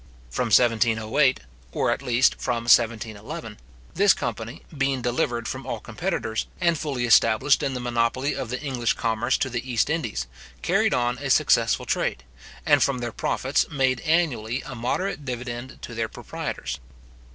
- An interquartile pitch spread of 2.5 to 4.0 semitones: Yes, average, 2.9 semitones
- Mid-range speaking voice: No, low, 125 Hz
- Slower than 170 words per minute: Yes, average, 155 wpm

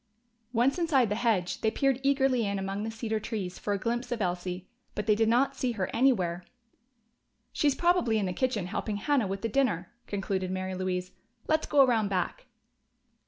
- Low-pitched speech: No, high, 220 Hz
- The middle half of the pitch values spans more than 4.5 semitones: Yes, average, 5.2 semitones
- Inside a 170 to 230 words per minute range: Yes, average, 185 wpm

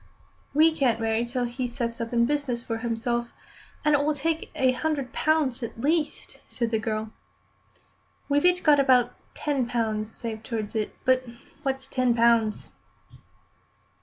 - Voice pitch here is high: Yes, high, 245 Hz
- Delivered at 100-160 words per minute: Yes, average, 155 wpm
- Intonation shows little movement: No, average, 3.8 semitones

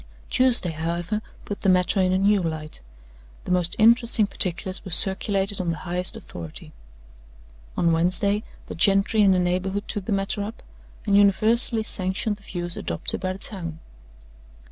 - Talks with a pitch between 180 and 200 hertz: Yes, high, 190 Hz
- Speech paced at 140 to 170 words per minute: Yes, average, 160 wpm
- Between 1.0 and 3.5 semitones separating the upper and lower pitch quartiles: Yes, average, 2.7 semitones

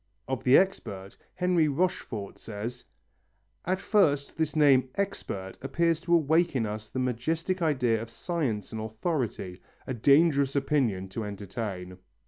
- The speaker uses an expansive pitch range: Yes, wide, 7.1 semitones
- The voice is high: No, low, 130 Hz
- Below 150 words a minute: Yes, slow, 135 wpm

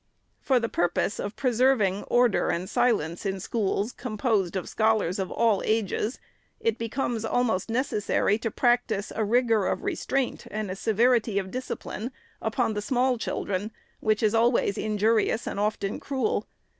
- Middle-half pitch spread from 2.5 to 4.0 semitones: Yes, average, 3.1 semitones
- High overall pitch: Yes, high, 220 Hz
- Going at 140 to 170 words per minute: Yes, average, 155 wpm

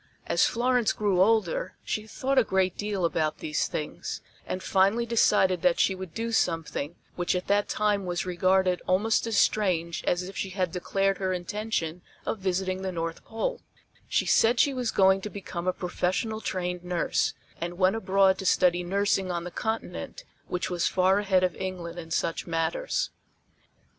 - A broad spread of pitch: No, average, 2.9 semitones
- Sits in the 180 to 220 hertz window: Yes, high, 190 Hz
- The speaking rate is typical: Yes, average, 175 wpm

